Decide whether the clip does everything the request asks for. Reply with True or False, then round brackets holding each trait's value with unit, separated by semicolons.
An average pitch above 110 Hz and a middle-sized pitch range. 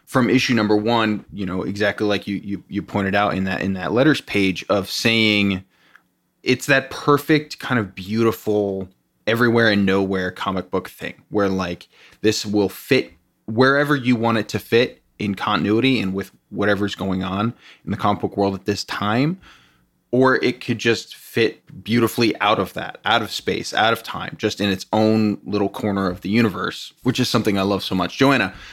False (105 Hz; 3.2 semitones)